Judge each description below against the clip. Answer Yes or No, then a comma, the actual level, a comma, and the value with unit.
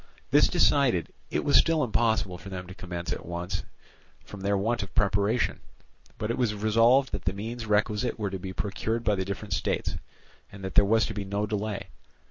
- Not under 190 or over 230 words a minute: Yes, average, 200 wpm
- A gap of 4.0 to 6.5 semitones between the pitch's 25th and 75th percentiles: No, average, 2.8 semitones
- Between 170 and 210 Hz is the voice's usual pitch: No, low, 105 Hz